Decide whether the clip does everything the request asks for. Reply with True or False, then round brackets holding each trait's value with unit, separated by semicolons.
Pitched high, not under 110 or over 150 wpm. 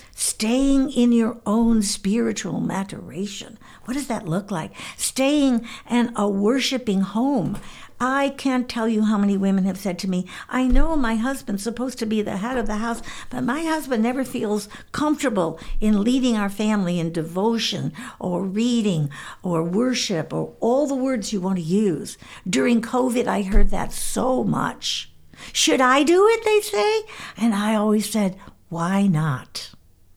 False (225 Hz; 165 wpm)